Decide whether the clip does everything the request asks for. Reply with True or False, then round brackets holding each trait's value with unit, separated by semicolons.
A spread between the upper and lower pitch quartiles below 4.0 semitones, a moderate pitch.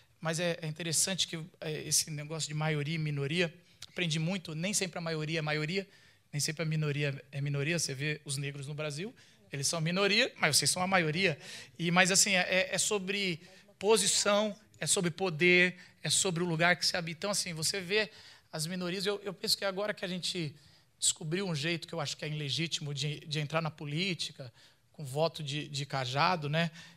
True (3.5 semitones; 165 Hz)